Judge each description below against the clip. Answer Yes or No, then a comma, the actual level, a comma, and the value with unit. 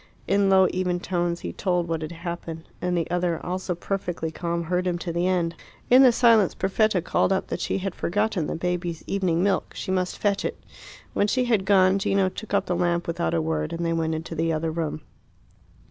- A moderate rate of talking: No, fast, 215 wpm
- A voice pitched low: No, medium, 180 Hz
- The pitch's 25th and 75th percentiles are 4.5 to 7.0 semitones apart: No, narrow, 2.5 semitones